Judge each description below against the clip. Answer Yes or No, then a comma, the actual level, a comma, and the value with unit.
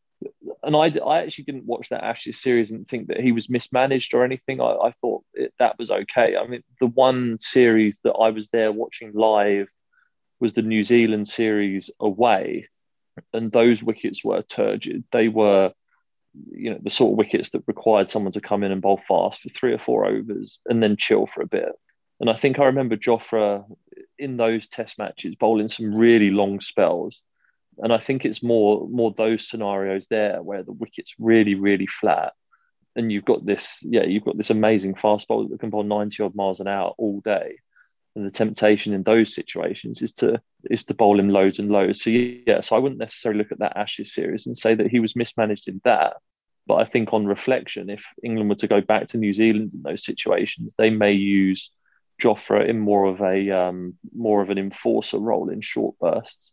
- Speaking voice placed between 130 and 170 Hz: No, low, 110 Hz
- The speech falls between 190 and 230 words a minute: Yes, fast, 205 wpm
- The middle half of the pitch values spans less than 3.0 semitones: Yes, narrow, 2.5 semitones